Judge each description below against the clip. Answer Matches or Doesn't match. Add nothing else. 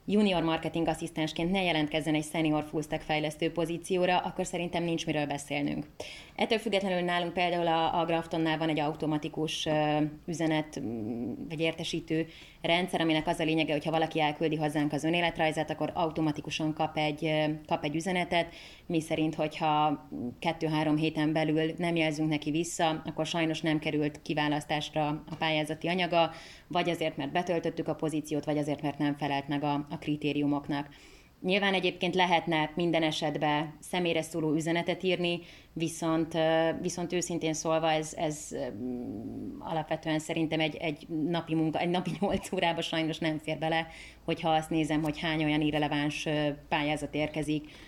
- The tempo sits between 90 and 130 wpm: Doesn't match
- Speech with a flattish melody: Matches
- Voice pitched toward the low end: Doesn't match